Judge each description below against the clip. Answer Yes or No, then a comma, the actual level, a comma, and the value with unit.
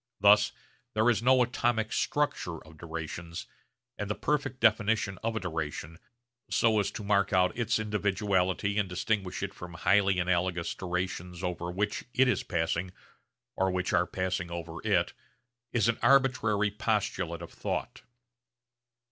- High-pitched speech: No, very low, 95 Hz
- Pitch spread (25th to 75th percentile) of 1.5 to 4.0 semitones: Yes, average, 3.7 semitones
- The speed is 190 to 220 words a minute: No, average, 145 wpm